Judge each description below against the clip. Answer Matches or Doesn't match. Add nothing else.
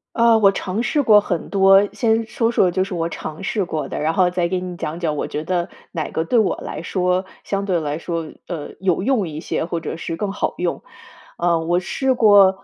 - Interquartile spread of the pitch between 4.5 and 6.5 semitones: Doesn't match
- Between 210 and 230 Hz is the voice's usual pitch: Doesn't match